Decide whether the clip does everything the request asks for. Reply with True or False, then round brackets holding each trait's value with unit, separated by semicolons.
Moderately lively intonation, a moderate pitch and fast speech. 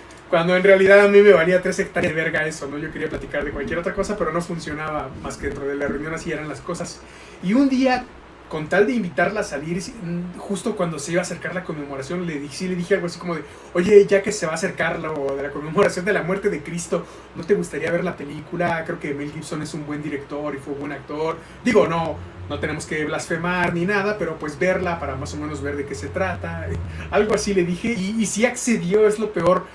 True (4.1 semitones; 170 Hz; 250 wpm)